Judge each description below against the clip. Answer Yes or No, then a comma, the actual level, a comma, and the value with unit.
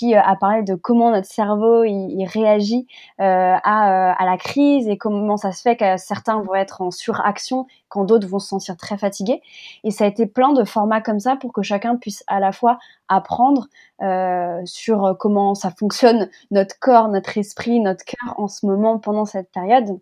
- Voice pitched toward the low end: No, high, 210 Hz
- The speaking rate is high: No, average, 200 wpm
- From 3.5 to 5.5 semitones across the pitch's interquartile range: No, average, 3.1 semitones